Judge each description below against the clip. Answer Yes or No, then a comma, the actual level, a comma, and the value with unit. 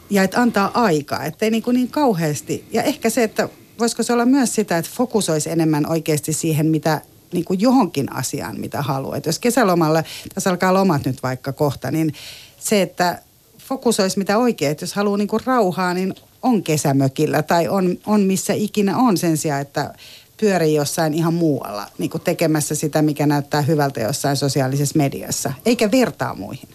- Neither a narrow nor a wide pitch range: No, wide, 6.1 semitones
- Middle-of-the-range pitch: Yes, medium, 165 Hz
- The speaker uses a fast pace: Yes, fast, 175 wpm